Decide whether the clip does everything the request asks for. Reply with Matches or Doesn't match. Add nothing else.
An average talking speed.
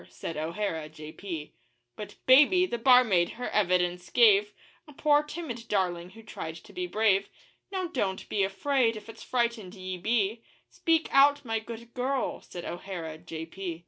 Matches